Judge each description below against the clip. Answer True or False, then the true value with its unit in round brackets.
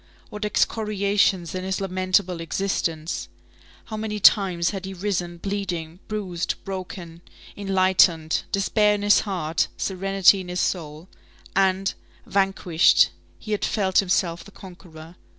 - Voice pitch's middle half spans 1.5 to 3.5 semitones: True (2.5 semitones)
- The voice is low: False (190 Hz)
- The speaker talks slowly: True (125 wpm)